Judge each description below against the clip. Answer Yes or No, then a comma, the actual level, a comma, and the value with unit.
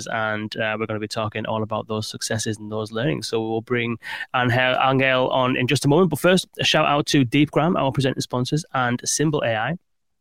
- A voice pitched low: Yes, low, 125 Hz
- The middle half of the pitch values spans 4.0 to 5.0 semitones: Yes, average, 4.6 semitones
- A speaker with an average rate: No, fast, 210 wpm